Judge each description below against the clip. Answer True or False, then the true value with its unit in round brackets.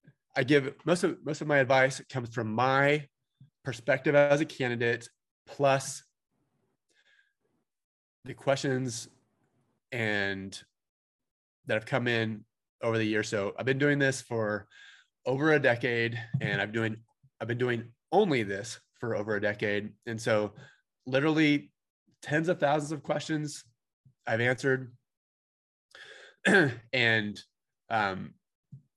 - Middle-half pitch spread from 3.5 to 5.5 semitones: True (4.0 semitones)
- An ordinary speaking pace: False (120 wpm)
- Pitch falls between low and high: False (130 Hz)